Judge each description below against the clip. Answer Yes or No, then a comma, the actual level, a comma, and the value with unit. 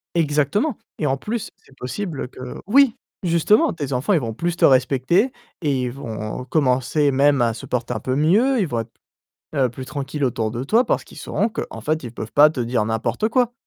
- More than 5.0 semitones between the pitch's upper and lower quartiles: Yes, wide, 5.6 semitones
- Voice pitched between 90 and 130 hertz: No, medium, 140 Hz